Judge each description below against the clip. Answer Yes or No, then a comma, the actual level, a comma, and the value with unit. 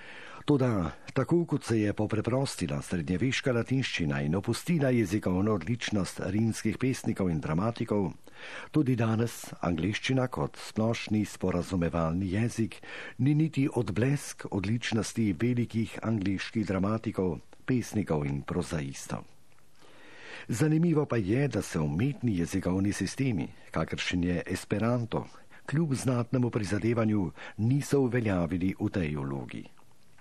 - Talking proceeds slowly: Yes, slow, 105 wpm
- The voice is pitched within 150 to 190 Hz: No, low, 110 Hz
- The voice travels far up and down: No, average, 5.0 semitones